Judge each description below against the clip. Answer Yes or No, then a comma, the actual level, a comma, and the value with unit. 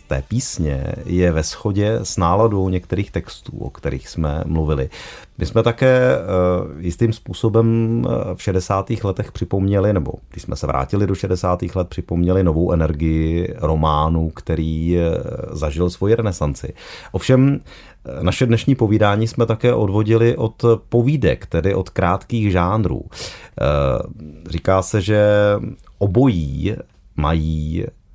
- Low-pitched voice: Yes, very low, 95 Hz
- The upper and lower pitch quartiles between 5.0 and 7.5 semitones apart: Yes, average, 5.3 semitones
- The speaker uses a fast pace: No, slow, 115 wpm